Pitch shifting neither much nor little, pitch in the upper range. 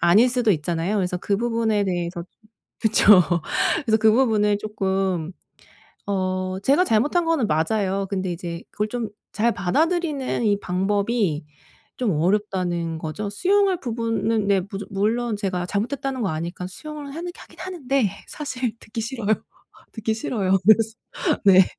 Yes: average, 4.3 semitones; high, 210 Hz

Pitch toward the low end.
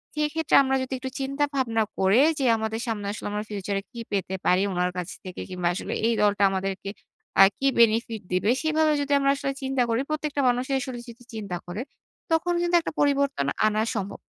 No: high, 230 Hz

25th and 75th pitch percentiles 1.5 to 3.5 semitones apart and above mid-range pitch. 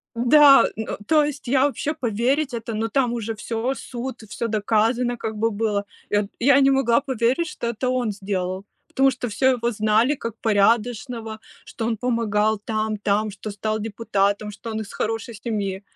Yes: average, 2.8 semitones; high, 225 Hz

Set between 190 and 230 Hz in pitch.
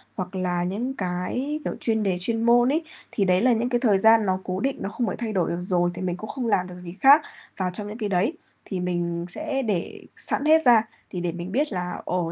Yes: high, 200 Hz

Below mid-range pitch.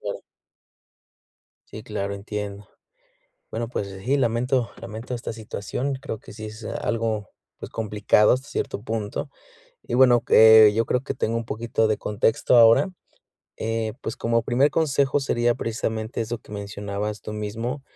Yes: low, 115 Hz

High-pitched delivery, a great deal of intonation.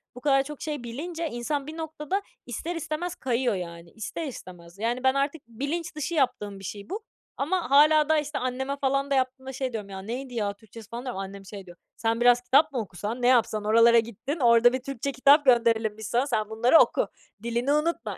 No: very high, 250 Hz; average, 4.4 semitones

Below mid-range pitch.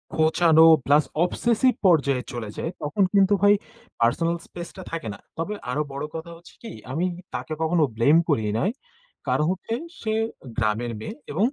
No: medium, 160 Hz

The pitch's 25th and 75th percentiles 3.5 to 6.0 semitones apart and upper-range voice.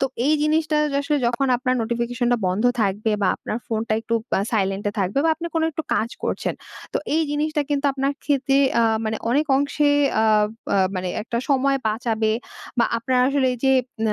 Yes: average, 4.5 semitones; high, 245 Hz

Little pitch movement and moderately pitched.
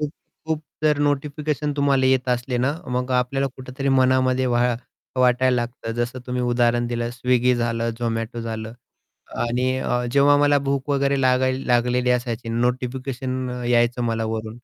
No: narrow, 1.8 semitones; low, 125 Hz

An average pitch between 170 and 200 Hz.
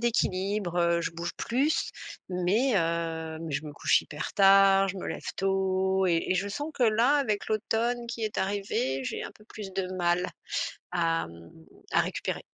Yes: high, 190 Hz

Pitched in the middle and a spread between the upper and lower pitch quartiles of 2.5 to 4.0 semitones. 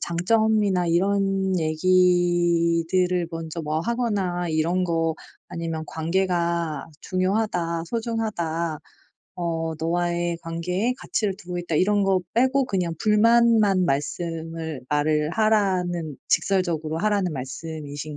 Yes: medium, 175 Hz; average, 3.0 semitones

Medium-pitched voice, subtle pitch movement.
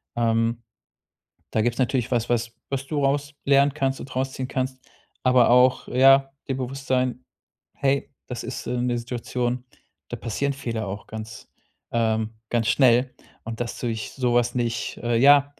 No: low, 125 Hz; narrow, 2.3 semitones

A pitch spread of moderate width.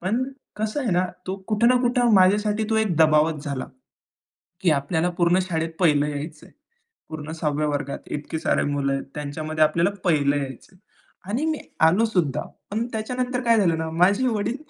No: wide, 6.1 semitones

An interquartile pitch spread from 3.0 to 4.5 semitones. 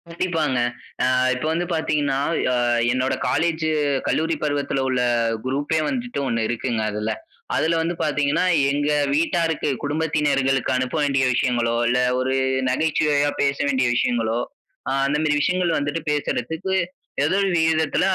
Yes: average, 3.7 semitones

